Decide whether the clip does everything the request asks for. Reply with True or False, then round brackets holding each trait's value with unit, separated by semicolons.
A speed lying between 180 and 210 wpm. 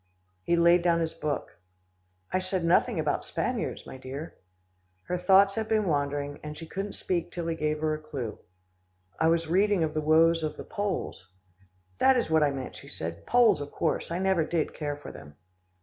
True (195 wpm)